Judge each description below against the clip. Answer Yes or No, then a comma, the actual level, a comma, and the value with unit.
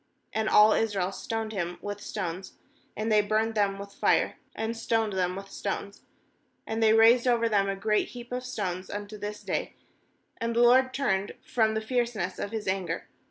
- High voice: Yes, high, 215 Hz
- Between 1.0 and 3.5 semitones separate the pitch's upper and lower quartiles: Yes, narrow, 2.4 semitones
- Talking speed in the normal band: Yes, average, 185 wpm